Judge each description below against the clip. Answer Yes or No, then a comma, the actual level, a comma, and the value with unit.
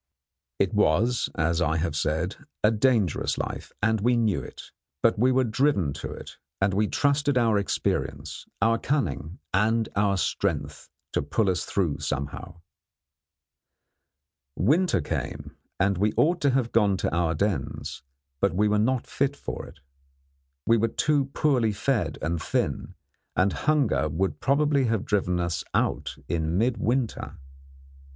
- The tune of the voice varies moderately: No, wide, 6.3 semitones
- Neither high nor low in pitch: No, low, 105 Hz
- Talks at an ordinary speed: Yes, average, 150 wpm